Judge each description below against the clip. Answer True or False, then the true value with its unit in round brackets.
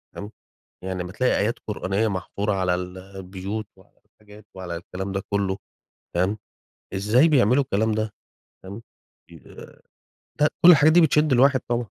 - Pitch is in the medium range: False (105 Hz)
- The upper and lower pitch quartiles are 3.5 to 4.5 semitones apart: True (4.2 semitones)